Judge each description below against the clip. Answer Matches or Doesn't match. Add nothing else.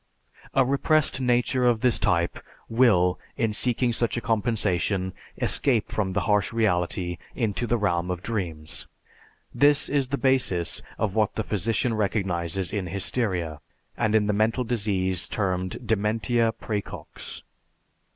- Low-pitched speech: Matches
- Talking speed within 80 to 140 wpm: Matches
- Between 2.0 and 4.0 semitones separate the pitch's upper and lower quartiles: Doesn't match